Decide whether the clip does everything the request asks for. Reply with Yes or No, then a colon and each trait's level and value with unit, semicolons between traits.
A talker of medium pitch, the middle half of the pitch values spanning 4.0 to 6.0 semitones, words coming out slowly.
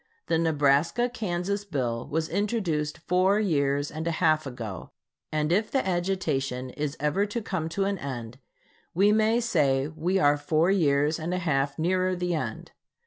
No: medium, 160 Hz; average, 4.9 semitones; average, 165 wpm